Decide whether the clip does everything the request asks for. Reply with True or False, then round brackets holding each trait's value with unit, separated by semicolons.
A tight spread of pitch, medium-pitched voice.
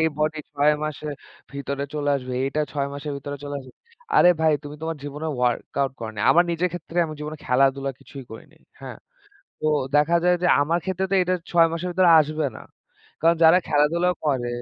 False (3.0 semitones; 150 Hz)